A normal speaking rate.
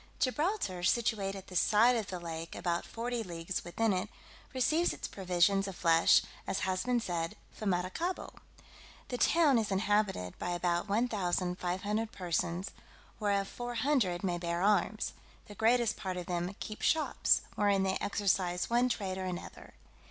Yes: average, 155 wpm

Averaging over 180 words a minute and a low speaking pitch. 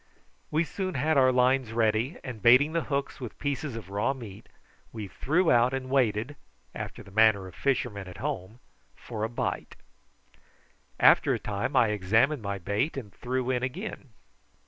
No: average, 170 wpm; low, 120 Hz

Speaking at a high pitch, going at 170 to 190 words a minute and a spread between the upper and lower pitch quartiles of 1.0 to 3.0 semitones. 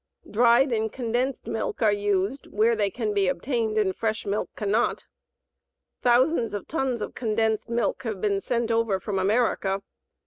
No: high, 220 Hz; average, 160 wpm; average, 2.7 semitones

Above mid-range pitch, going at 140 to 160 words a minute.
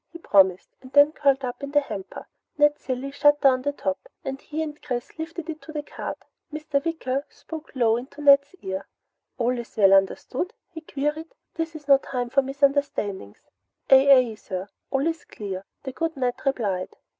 No: very high, 275 Hz; average, 185 wpm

